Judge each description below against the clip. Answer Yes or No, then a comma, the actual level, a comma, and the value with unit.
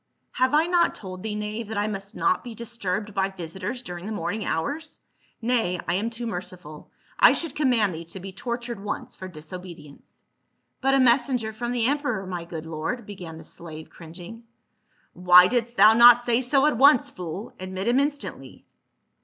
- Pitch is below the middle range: No, high, 210 Hz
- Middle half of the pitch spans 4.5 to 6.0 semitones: Yes, average, 5.0 semitones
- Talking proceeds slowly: No, average, 190 wpm